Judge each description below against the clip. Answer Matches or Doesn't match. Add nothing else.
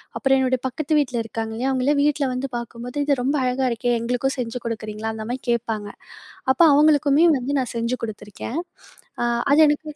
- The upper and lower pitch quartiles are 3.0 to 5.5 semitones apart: Matches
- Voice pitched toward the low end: Doesn't match